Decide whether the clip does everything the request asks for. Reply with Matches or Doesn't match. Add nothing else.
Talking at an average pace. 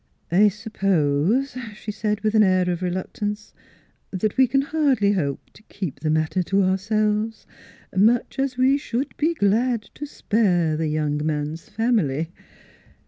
Matches